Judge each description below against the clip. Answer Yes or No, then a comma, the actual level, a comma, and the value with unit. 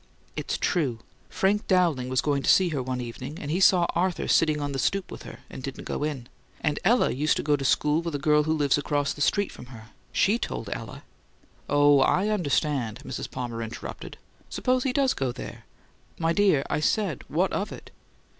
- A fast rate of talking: Yes, fast, 210 wpm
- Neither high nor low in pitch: Yes, medium, 150 Hz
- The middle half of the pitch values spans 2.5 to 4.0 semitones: No, average, 5.1 semitones